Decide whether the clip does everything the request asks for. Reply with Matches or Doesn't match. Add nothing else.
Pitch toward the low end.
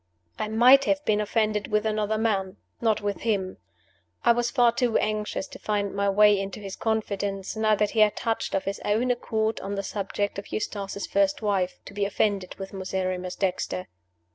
Doesn't match